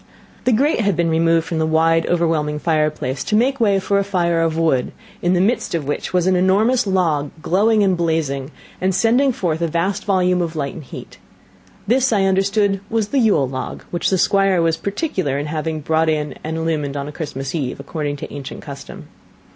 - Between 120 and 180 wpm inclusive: No, average, 200 wpm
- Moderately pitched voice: Yes, medium, 170 Hz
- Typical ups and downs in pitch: Yes, average, 4.3 semitones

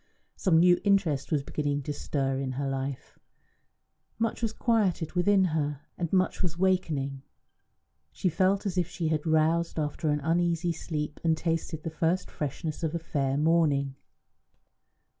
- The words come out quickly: No, average, 155 wpm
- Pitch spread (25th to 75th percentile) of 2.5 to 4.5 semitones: Yes, average, 3.3 semitones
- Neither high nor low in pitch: Yes, medium, 160 Hz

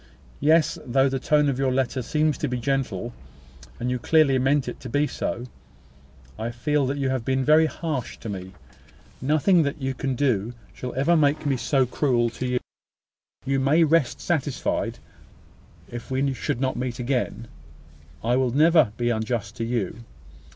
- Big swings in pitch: No, average, 3.1 semitones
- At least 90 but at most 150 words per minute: No, average, 175 wpm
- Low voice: Yes, low, 130 Hz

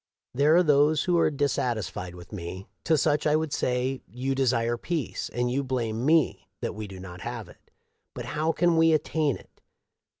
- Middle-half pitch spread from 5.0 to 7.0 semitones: Yes, average, 5.3 semitones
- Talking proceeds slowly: No, average, 195 wpm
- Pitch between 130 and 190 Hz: Yes, low, 135 Hz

